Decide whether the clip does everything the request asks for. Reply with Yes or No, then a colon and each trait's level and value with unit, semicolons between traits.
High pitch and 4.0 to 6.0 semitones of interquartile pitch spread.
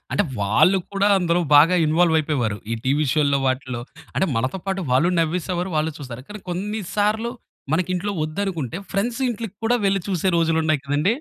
No: medium, 170 Hz; average, 4.9 semitones